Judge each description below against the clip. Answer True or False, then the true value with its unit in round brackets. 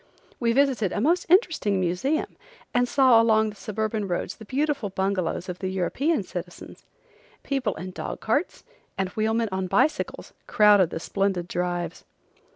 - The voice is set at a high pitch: True (210 Hz)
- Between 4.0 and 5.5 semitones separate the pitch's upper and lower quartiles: True (4.9 semitones)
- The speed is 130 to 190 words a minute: True (150 wpm)